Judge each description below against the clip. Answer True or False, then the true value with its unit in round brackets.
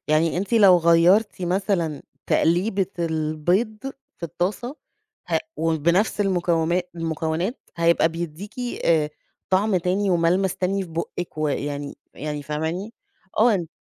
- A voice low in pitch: False (170 Hz)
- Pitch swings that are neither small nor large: True (3.3 semitones)